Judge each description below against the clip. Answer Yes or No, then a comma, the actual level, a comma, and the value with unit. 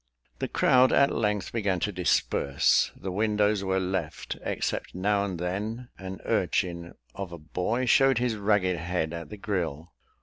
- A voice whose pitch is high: No, very low, 95 Hz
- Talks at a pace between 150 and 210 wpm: Yes, average, 160 wpm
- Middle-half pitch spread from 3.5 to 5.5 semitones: No, average, 3.1 semitones